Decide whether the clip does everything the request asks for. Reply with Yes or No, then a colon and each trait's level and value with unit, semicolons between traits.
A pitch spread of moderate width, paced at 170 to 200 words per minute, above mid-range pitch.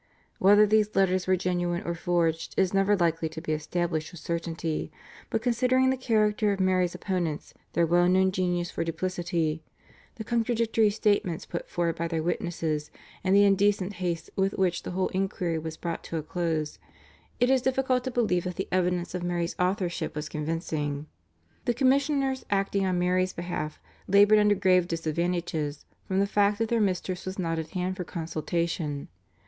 No: average, 3.2 semitones; average, 175 wpm; medium, 180 Hz